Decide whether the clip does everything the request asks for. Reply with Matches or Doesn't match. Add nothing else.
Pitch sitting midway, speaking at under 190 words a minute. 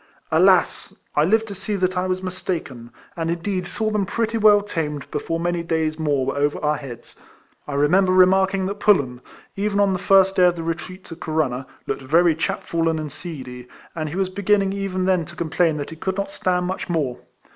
Doesn't match